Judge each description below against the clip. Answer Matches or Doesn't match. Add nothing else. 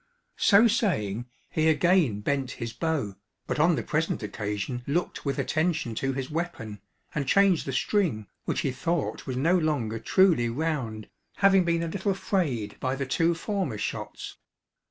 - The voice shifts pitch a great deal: Matches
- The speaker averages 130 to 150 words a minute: Doesn't match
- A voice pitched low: Doesn't match